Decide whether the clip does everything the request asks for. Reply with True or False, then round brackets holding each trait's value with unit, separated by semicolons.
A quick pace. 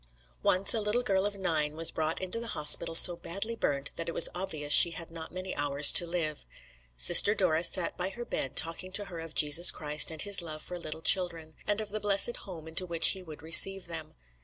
True (225 wpm)